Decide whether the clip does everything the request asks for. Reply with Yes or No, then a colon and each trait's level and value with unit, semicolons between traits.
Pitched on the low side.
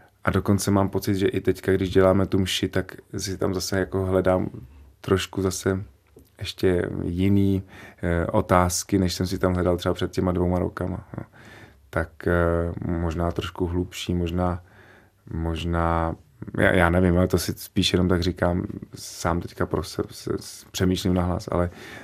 Yes: very low, 95 Hz